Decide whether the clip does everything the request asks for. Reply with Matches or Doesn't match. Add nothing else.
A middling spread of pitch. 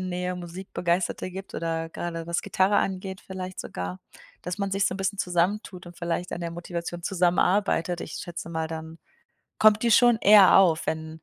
Doesn't match